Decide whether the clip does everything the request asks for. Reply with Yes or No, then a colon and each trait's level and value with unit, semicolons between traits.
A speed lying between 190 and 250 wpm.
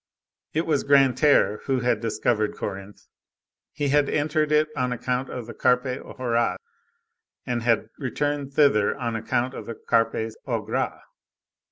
No: average, 145 wpm